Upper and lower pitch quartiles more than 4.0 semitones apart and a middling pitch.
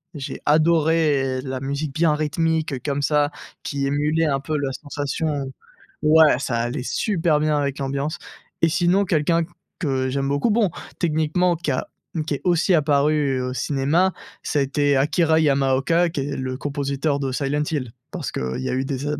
No: average, 2.7 semitones; medium, 145 Hz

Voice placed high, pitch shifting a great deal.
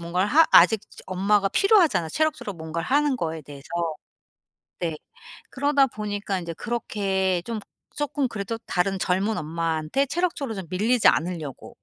Yes: high, 200 Hz; wide, 7.3 semitones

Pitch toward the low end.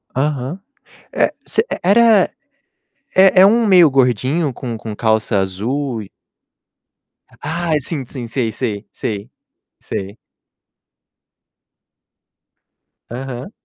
Yes: low, 130 Hz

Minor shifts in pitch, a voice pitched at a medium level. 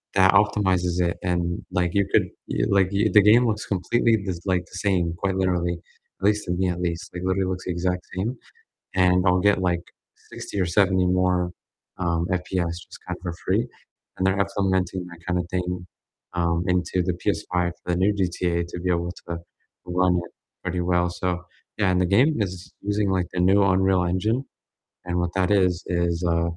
No: narrow, 1.5 semitones; very low, 90 Hz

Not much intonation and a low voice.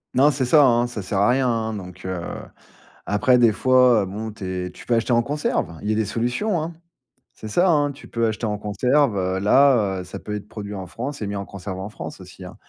No: average, 4.1 semitones; low, 110 Hz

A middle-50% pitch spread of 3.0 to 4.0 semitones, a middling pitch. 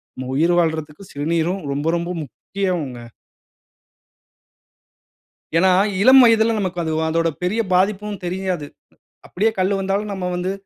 Yes: average, 3.4 semitones; medium, 180 Hz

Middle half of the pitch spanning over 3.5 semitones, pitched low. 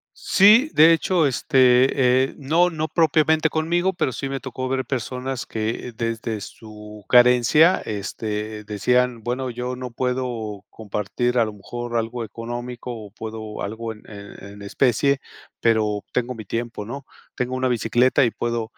No: average, 3.2 semitones; low, 120 Hz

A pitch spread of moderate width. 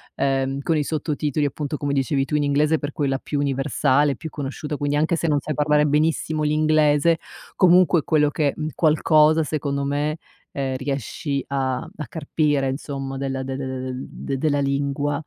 No: narrow, 1.9 semitones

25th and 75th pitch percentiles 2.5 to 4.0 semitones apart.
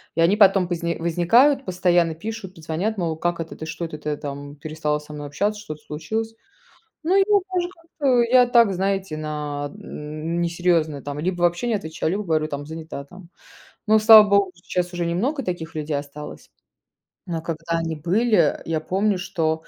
No: average, 4.6 semitones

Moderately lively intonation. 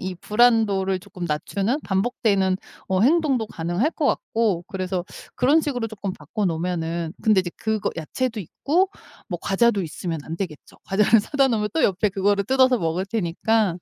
Yes: average, 4.3 semitones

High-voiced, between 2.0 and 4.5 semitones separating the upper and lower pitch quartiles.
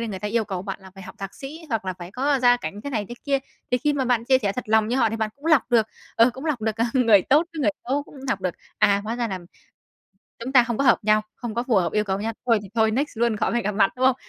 Yes: high, 230 Hz; average, 3.8 semitones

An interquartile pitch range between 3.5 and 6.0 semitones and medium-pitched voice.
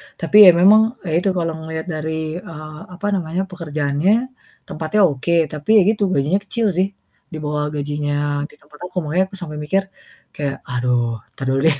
Yes: average, 4.2 semitones; medium, 160 Hz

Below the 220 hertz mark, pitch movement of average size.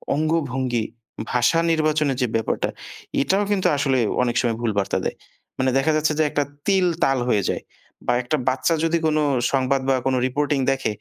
Yes: low, 135 Hz; average, 3.7 semitones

